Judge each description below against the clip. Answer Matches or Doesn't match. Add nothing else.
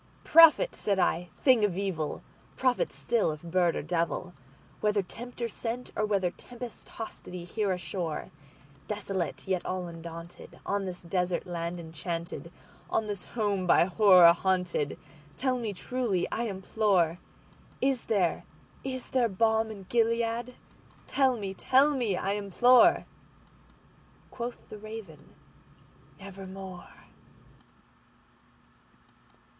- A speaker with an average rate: Doesn't match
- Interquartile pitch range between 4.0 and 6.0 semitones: Matches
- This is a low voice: Doesn't match